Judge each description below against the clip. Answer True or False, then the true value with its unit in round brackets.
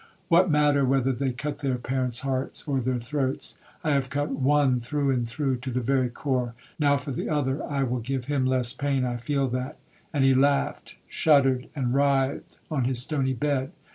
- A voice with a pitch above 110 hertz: True (135 Hz)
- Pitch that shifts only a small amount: True (2.0 semitones)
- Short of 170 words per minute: False (185 wpm)